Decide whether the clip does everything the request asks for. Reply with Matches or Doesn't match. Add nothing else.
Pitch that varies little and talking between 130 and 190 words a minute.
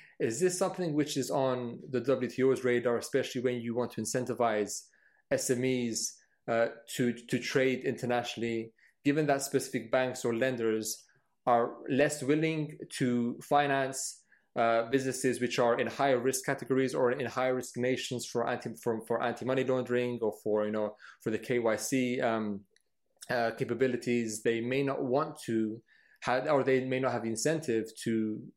Matches